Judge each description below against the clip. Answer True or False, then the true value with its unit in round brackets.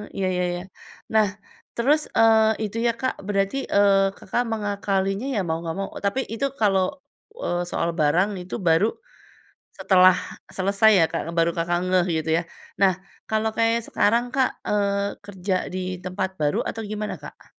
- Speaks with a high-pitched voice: True (200 Hz)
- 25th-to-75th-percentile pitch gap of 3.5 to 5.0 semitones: False (3.1 semitones)